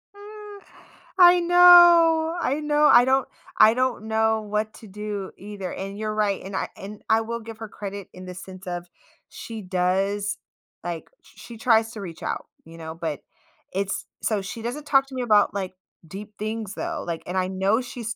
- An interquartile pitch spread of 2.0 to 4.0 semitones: No, average, 4.8 semitones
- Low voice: No, high, 215 Hz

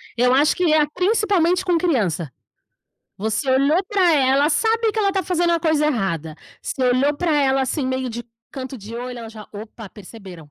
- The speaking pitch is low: No, very high, 270 Hz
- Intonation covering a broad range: Yes, wide, 6.8 semitones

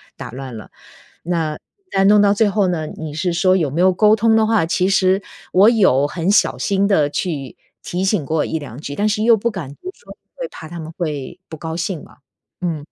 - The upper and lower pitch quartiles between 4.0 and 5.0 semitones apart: Yes, average, 4.7 semitones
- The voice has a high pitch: No, medium, 180 Hz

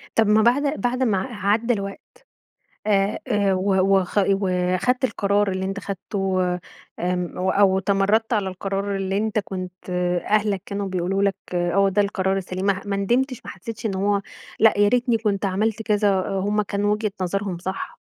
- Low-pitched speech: No, high, 200 Hz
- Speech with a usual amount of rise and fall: No, narrow, 1.8 semitones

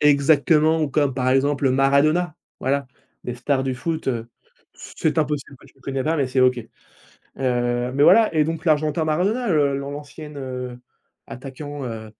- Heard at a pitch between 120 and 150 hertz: Yes, medium, 140 Hz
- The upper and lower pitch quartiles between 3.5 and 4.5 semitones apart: No, average, 2.9 semitones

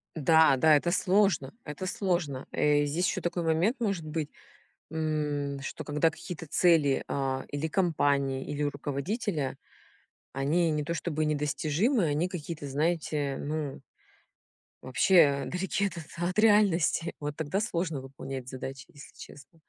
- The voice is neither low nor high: Yes, medium, 155 Hz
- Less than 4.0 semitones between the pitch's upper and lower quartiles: Yes, average, 3.5 semitones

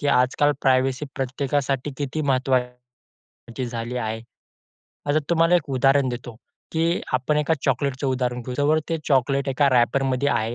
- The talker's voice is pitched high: No, low, 135 Hz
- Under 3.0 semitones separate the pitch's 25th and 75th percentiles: Yes, narrow, 2.5 semitones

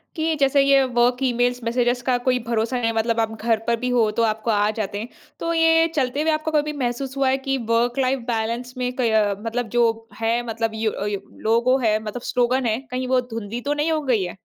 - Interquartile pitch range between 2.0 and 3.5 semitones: Yes, average, 2.8 semitones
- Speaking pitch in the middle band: No, high, 245 Hz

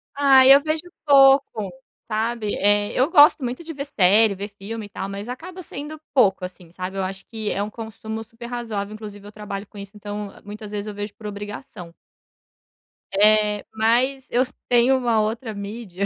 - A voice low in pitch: No, high, 215 Hz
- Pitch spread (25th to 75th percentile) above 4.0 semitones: No, average, 3.5 semitones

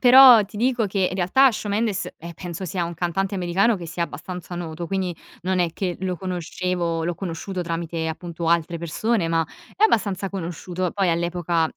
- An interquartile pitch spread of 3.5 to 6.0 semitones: No, narrow, 2.4 semitones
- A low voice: No, medium, 180 Hz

